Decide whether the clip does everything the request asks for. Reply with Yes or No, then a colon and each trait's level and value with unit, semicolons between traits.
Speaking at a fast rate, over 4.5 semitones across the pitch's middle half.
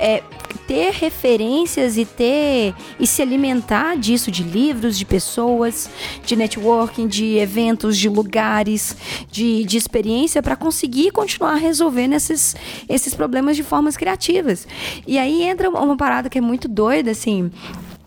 No: average, 140 wpm; average, 5.2 semitones